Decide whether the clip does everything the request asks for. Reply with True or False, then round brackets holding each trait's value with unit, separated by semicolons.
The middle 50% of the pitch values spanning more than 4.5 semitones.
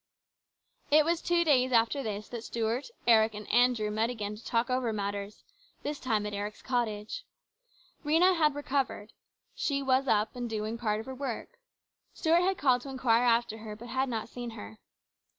False (3.9 semitones)